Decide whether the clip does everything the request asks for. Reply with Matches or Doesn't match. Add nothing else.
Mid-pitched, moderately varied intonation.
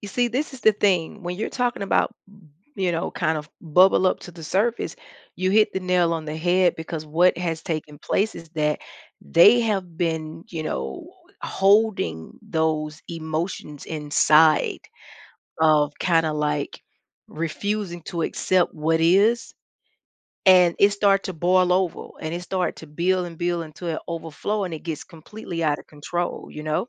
Matches